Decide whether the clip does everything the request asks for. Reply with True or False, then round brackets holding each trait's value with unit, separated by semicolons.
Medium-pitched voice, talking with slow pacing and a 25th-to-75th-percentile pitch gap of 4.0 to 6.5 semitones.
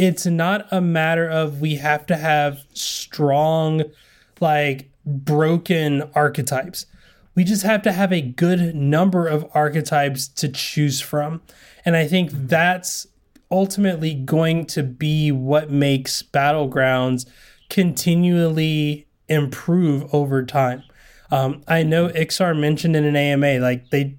False (150 Hz; 125 wpm; 2.9 semitones)